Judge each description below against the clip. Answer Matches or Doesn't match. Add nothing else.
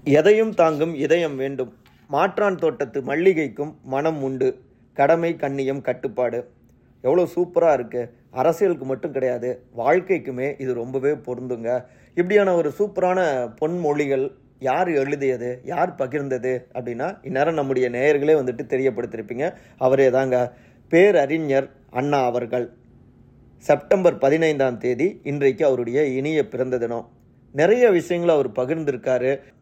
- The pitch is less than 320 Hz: Matches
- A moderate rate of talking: Matches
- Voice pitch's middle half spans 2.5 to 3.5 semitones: Doesn't match